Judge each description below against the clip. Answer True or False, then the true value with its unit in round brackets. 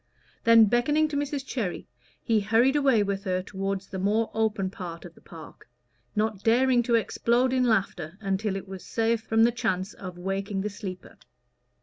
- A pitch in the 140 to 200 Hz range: False (215 Hz)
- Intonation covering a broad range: False (3.5 semitones)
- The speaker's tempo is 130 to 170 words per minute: False (180 wpm)